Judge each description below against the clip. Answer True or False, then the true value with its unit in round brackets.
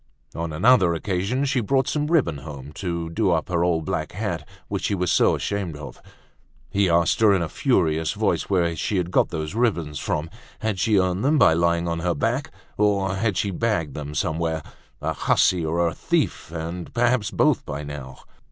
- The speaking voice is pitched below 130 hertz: True (85 Hz)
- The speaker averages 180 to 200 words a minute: True (195 wpm)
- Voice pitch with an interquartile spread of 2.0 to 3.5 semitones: False (4.2 semitones)